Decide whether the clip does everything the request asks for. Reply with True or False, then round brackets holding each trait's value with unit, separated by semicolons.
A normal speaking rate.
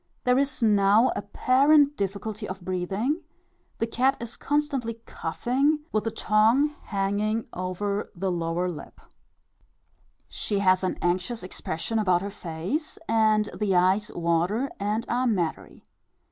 False (130 wpm)